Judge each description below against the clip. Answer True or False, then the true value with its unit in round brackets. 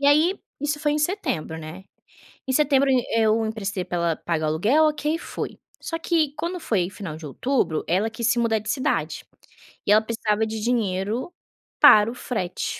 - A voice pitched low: False (225 Hz)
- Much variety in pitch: True (7.1 semitones)